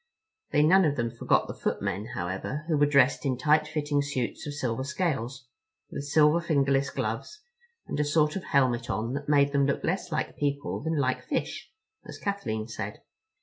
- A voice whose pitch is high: No, medium, 140 Hz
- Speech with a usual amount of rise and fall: Yes, average, 3.3 semitones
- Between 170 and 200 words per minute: Yes, average, 185 wpm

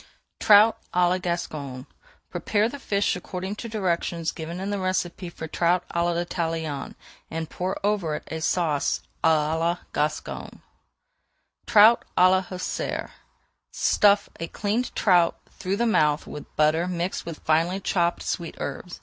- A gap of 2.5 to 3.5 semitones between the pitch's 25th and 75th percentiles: Yes, average, 2.9 semitones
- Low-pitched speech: No, medium, 175 Hz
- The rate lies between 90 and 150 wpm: Yes, average, 145 wpm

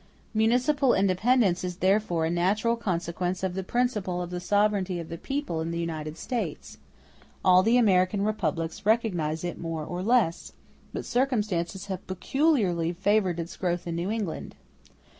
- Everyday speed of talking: Yes, average, 155 wpm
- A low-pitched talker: No, medium, 185 Hz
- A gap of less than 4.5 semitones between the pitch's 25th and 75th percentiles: Yes, average, 4.0 semitones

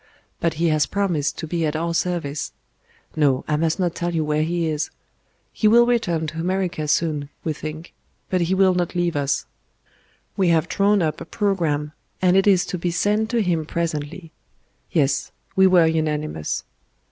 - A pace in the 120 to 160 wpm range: No, average, 180 wpm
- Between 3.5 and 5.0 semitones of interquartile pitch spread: No, average, 3.1 semitones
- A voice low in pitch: No, medium, 165 Hz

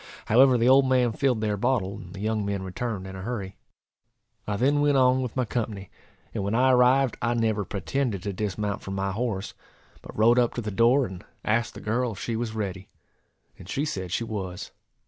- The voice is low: Yes, low, 110 Hz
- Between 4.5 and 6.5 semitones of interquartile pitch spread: No, average, 4.0 semitones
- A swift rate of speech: Yes, fast, 210 wpm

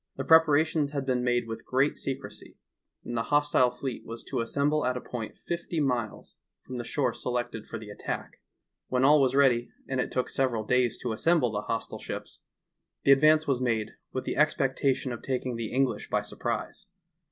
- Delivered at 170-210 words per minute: Yes, average, 190 wpm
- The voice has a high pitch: No, low, 130 Hz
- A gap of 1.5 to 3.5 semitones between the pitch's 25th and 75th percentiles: Yes, average, 2.8 semitones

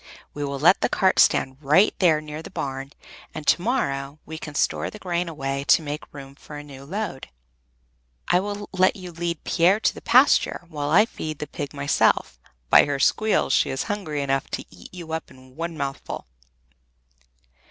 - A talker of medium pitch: Yes, medium, 155 Hz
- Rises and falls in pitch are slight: No, average, 4.4 semitones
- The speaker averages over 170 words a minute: Yes, average, 190 wpm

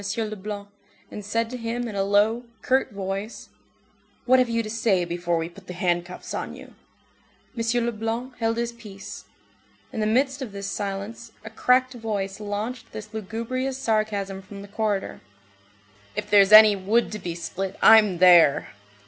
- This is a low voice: No, high, 215 Hz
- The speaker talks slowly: No, average, 165 wpm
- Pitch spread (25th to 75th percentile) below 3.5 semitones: Yes, average, 2.9 semitones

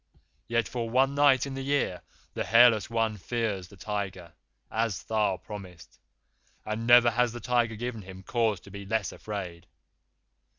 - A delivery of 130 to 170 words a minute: Yes, average, 160 wpm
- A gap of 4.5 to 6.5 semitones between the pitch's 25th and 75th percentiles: No, average, 3.4 semitones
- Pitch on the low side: Yes, low, 110 Hz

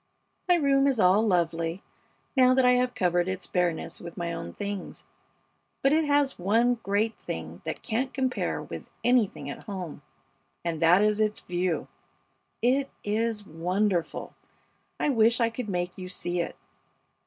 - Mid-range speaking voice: No, high, 205 Hz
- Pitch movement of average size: No, wide, 5.9 semitones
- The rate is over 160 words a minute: No, average, 155 wpm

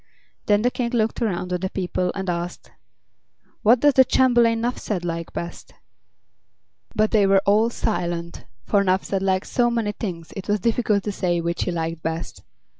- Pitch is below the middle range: No, high, 195 Hz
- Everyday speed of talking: Yes, average, 175 wpm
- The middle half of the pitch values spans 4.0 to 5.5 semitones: Yes, average, 4.5 semitones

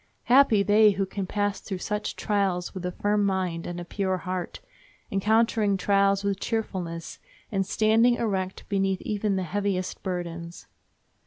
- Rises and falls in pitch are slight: Yes, narrow, 2.2 semitones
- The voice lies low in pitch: No, high, 195 Hz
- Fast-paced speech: No, average, 150 wpm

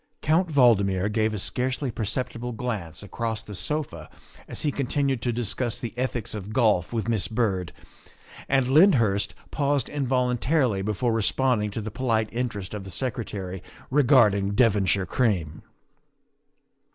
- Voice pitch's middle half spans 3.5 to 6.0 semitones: Yes, average, 4.2 semitones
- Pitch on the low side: Yes, low, 115 Hz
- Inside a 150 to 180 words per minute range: No, average, 140 wpm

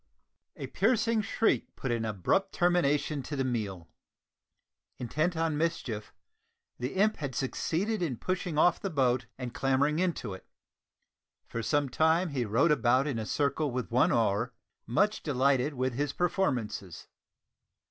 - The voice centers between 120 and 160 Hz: Yes, medium, 140 Hz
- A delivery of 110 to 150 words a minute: Yes, average, 145 wpm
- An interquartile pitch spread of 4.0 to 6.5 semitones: Yes, wide, 5.6 semitones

